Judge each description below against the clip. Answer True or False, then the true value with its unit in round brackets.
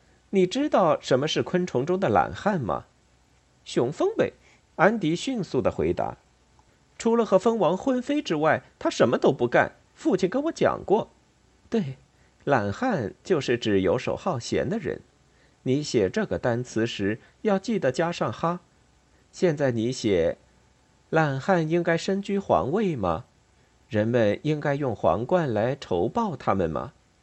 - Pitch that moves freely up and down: True (8.6 semitones)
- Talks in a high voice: False (160 Hz)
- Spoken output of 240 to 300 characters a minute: False (210 characters per minute)